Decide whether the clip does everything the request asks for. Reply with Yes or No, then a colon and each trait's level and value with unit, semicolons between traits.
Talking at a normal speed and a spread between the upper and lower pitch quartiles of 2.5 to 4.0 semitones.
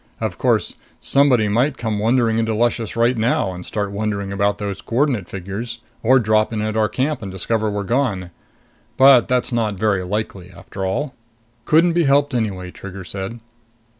Yes: average, 170 wpm; average, 3.7 semitones